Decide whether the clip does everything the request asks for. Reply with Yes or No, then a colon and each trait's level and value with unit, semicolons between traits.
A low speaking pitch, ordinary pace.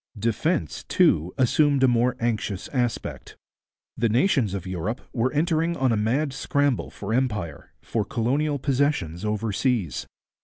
No: low, 120 Hz; slow, 130 wpm